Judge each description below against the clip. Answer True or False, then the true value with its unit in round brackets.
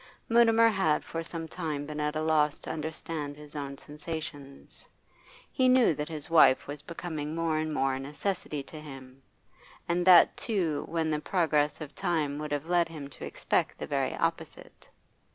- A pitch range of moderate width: False (2.2 semitones)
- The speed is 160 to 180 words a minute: True (175 wpm)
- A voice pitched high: False (155 Hz)